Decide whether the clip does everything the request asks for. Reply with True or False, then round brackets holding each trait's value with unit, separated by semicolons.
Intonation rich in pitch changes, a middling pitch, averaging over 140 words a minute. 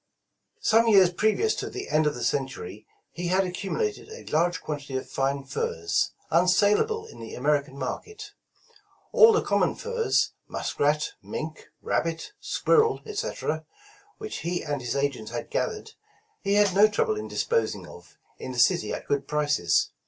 True (8.0 semitones; 165 Hz; 155 wpm)